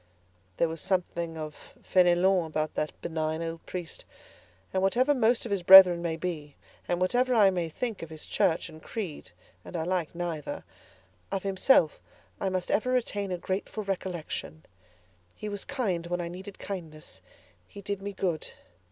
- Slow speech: No, average, 165 wpm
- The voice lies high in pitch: No, medium, 180 Hz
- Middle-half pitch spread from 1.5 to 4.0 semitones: Yes, average, 3.3 semitones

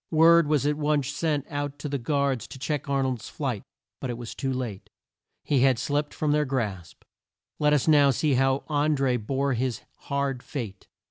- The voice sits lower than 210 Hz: Yes, medium, 140 Hz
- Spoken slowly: No, average, 195 wpm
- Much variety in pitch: No, narrow, 2.5 semitones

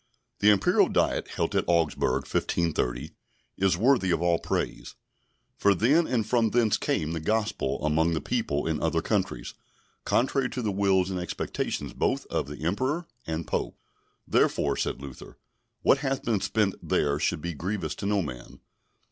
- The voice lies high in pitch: No, very low, 95 Hz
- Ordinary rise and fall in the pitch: No, wide, 5.8 semitones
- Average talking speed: Yes, average, 160 wpm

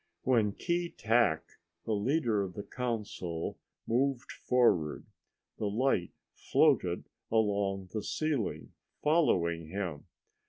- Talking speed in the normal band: No, slow, 95 wpm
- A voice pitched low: Yes, low, 110 Hz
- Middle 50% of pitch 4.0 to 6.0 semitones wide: Yes, average, 5.1 semitones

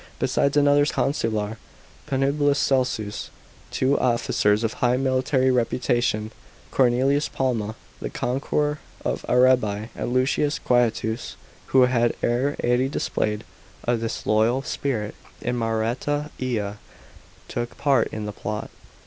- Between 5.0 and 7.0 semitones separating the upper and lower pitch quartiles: No, average, 3.2 semitones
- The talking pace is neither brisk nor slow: No, slow, 115 wpm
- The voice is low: Yes, low, 125 Hz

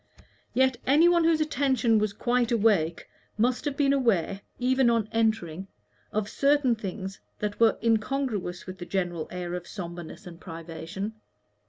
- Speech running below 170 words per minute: Yes, average, 150 wpm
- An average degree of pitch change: No, wide, 6.0 semitones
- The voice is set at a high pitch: Yes, high, 220 Hz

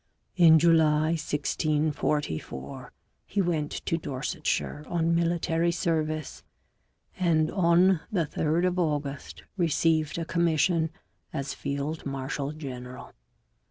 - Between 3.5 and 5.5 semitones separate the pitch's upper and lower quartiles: No, narrow, 2.4 semitones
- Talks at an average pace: No, slow, 100 wpm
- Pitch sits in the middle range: Yes, medium, 155 Hz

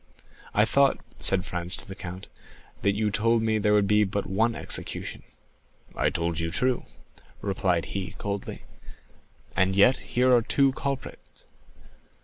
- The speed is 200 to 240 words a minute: No, average, 145 wpm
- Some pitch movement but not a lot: Yes, average, 3.4 semitones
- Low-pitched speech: Yes, low, 105 Hz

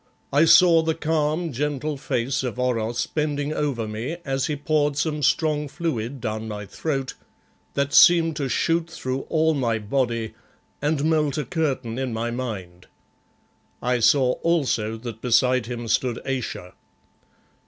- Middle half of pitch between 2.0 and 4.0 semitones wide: No, average, 4.5 semitones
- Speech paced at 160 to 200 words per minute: No, average, 145 wpm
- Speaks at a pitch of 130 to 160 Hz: Yes, low, 135 Hz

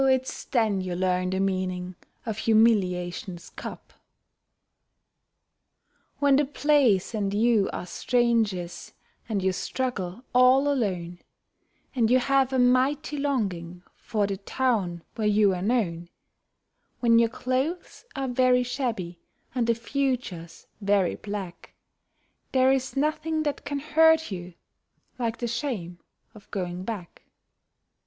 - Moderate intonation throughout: No, wide, 5.8 semitones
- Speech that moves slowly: Yes, slow, 125 wpm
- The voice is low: No, high, 225 Hz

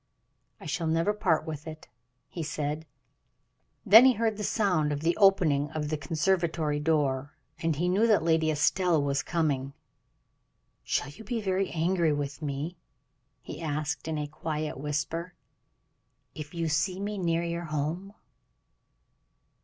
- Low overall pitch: No, medium, 160 Hz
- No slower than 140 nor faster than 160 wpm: Yes, average, 145 wpm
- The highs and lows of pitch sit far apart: No, average, 3.4 semitones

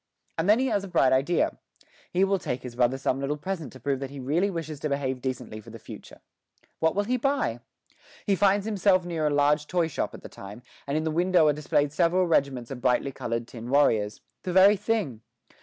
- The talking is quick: Yes, fast, 225 wpm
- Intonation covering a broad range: Yes, wide, 6.1 semitones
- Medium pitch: Yes, medium, 150 Hz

